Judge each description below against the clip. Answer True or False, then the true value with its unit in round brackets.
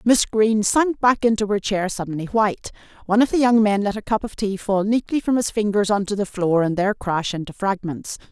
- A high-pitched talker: True (205 Hz)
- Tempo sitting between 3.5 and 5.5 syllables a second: False (5.7 syllables/s)